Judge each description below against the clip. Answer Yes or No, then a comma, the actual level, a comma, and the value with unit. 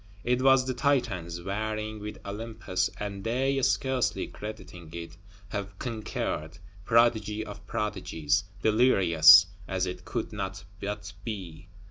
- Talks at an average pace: No, slow, 120 wpm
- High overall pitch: No, low, 105 Hz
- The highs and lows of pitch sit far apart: No, average, 3.9 semitones